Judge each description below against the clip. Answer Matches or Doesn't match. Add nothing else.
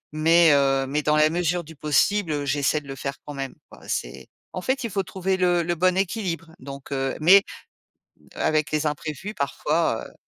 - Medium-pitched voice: Matches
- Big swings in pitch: Doesn't match